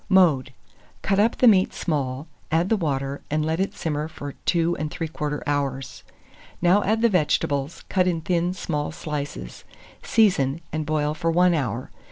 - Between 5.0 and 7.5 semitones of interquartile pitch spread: No, average, 4.0 semitones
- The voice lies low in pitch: No, medium, 155 Hz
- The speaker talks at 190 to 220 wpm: No, average, 155 wpm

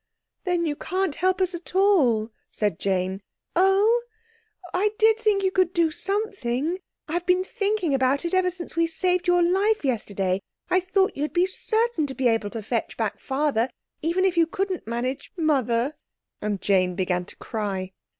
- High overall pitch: Yes, very high, 340 Hz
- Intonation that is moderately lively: No, wide, 8.3 semitones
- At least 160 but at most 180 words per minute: Yes, average, 170 wpm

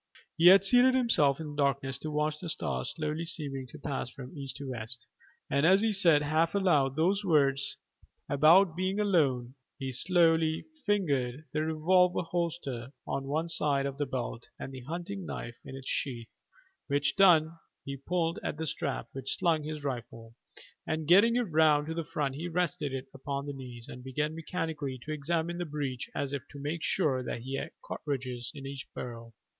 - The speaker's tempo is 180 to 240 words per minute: Yes, average, 185 wpm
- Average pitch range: Yes, average, 3.7 semitones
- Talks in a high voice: No, medium, 150 Hz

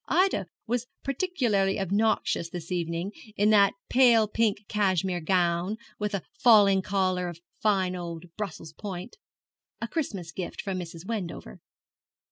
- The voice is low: No, high, 195 Hz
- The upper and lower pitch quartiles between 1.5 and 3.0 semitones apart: No, average, 3.5 semitones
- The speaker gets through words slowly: Yes, slow, 130 wpm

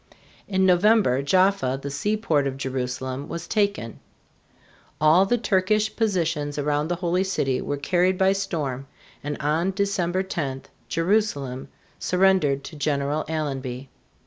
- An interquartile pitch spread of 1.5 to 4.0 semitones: No, wide, 5.4 semitones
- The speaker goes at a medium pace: No, slow, 125 wpm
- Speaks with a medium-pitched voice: Yes, medium, 160 Hz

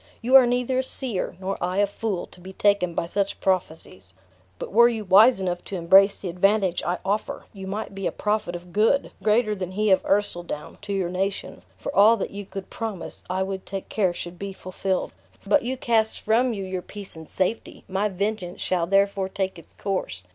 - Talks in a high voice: Yes, high, 195 Hz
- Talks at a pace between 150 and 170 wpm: No, fast, 205 wpm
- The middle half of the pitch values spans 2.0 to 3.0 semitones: Yes, narrow, 2.5 semitones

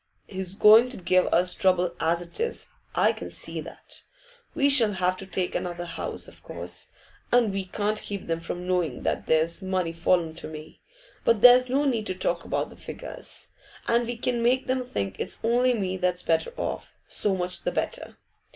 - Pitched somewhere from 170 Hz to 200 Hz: Yes, high, 190 Hz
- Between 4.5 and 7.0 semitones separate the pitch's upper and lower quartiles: Yes, average, 5.2 semitones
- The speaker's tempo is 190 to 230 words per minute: Yes, average, 195 wpm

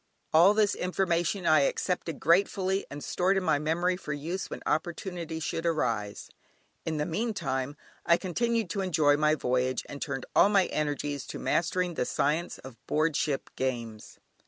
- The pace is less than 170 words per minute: Yes, average, 160 wpm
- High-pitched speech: No, medium, 160 Hz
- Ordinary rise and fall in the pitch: Yes, average, 4.0 semitones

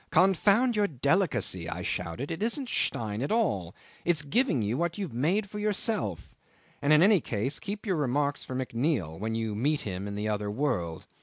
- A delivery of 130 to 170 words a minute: No, average, 190 wpm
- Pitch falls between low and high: Yes, medium, 145 Hz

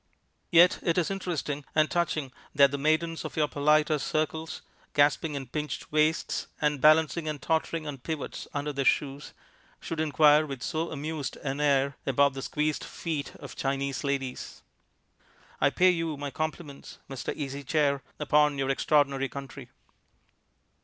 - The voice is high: No, medium, 150 Hz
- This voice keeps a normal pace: Yes, average, 150 wpm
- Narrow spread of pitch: Yes, narrow, 2.1 semitones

